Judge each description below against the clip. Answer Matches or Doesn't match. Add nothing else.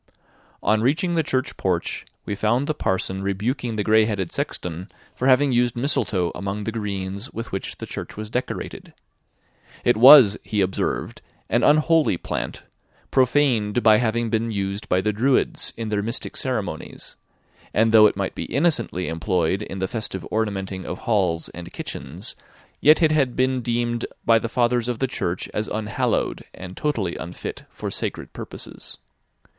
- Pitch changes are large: Doesn't match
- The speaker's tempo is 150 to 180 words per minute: Matches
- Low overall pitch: Matches